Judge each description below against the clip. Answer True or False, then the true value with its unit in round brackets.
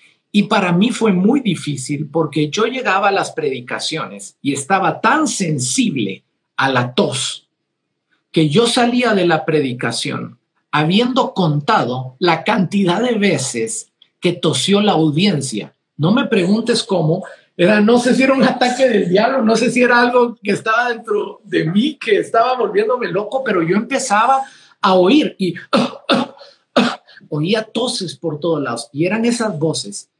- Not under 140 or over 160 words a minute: True (155 wpm)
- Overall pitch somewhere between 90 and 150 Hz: False (205 Hz)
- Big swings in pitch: True (7.0 semitones)